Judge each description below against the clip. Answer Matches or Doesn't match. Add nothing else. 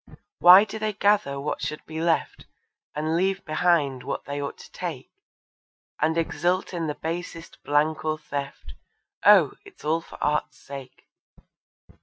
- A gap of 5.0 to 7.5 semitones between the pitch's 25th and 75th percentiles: Doesn't match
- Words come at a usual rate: Matches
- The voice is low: Doesn't match